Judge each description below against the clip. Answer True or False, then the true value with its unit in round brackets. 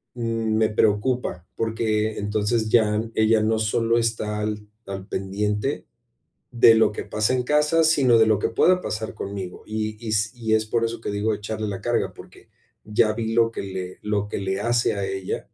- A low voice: True (110 Hz)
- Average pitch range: False (1.7 semitones)